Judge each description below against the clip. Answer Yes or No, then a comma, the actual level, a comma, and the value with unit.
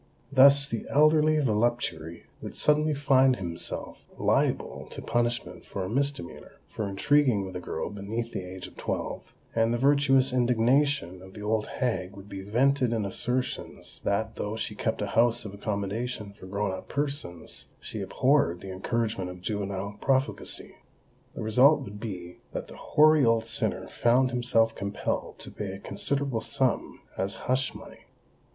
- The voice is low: Yes, low, 115 Hz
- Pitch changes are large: No, average, 5.0 semitones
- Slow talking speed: No, average, 160 wpm